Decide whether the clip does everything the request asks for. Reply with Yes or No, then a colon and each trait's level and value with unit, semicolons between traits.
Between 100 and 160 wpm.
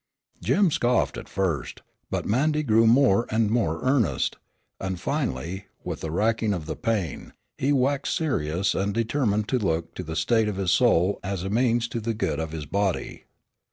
No: average, 180 wpm